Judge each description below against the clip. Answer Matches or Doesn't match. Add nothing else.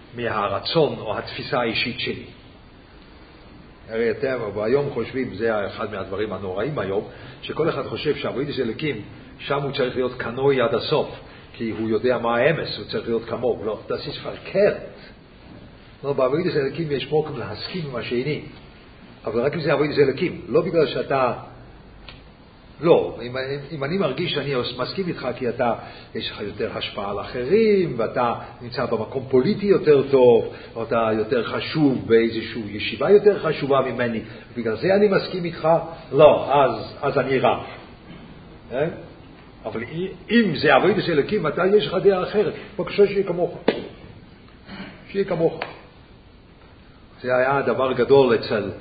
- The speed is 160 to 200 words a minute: Doesn't match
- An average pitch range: Doesn't match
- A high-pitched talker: Doesn't match